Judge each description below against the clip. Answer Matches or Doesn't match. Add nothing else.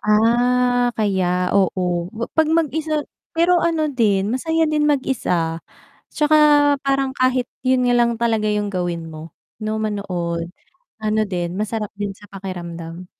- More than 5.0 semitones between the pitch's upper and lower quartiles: Matches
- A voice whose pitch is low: Doesn't match